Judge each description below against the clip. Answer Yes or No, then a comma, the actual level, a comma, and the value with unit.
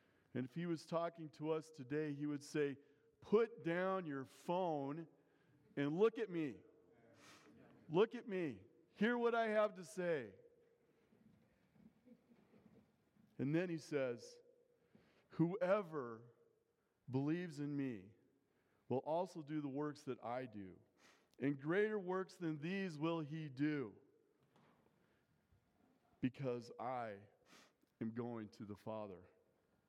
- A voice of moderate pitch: Yes, medium, 155 Hz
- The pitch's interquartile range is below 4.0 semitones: No, average, 5.3 semitones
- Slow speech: Yes, slow, 120 wpm